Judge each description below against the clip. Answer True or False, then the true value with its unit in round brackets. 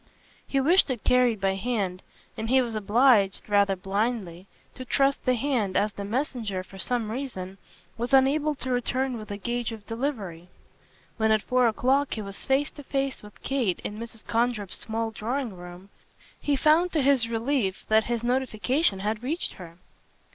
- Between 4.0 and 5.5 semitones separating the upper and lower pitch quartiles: True (4.5 semitones)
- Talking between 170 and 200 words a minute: True (175 wpm)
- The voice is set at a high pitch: True (230 Hz)